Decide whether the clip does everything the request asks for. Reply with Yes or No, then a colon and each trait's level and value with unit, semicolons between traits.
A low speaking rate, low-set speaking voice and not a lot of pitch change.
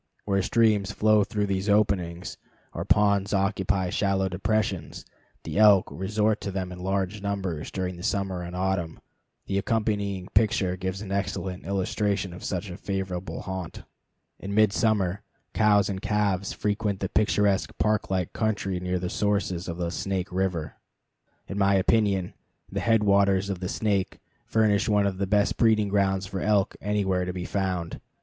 No: average, 160 wpm; low, 100 Hz; narrow, 1.8 semitones